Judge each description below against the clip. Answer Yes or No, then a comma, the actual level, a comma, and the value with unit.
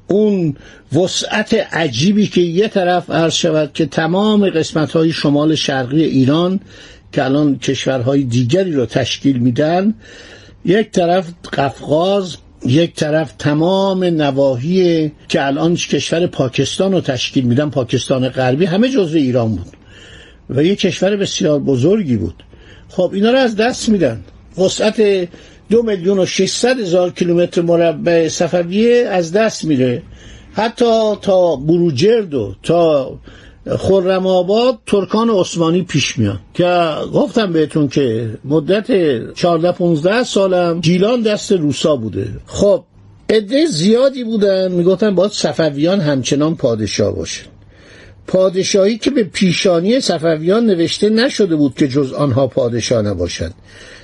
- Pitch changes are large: Yes, wide, 5.9 semitones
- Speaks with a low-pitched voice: No, medium, 170 Hz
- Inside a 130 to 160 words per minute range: No, average, 120 wpm